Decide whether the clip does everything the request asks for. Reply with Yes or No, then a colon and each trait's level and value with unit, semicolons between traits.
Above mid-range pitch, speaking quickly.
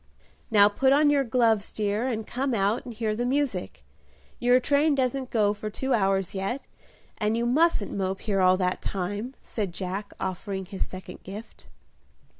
No: high, 215 Hz; average, 170 wpm